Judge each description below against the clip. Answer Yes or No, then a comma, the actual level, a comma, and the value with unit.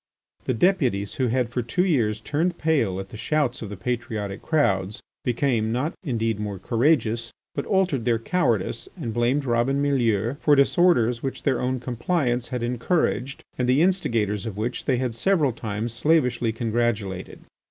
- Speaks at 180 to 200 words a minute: No, average, 165 wpm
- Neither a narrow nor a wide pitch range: Yes, average, 4.0 semitones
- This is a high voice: No, low, 120 Hz